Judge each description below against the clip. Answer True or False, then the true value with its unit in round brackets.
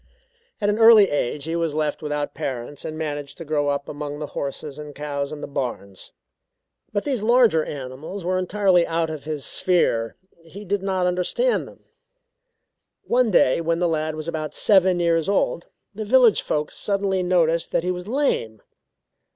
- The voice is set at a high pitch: False (165 Hz)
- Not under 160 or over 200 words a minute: True (175 wpm)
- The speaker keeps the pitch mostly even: False (4.7 semitones)